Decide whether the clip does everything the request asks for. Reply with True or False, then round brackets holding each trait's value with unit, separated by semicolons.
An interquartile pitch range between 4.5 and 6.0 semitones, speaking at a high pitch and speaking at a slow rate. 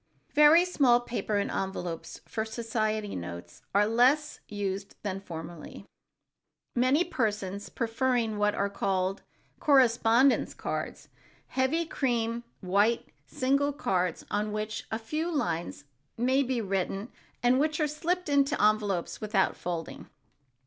True (4.9 semitones; 225 Hz; 125 wpm)